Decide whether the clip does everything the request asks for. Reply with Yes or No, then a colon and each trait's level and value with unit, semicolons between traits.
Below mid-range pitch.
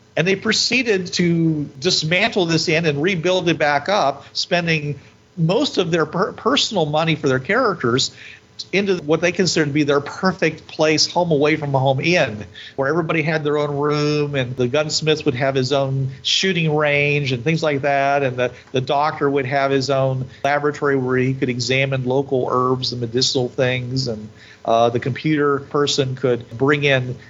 No: medium, 145 Hz